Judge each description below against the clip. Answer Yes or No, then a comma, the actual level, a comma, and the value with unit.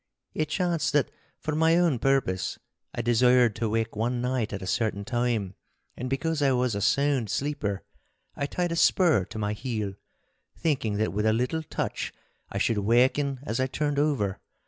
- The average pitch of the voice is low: Yes, low, 125 Hz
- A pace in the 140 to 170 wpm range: No, average, 180 wpm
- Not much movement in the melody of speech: No, average, 5.0 semitones